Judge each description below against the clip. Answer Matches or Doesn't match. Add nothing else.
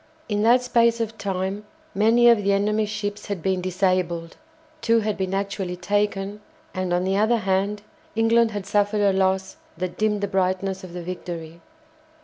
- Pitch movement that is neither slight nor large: Doesn't match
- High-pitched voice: Matches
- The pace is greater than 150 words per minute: Matches